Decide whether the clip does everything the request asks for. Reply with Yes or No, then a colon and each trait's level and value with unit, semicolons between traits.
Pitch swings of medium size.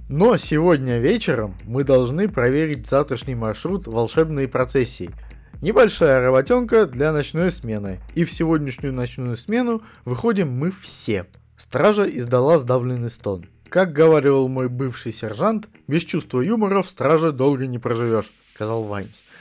No: wide, 5.7 semitones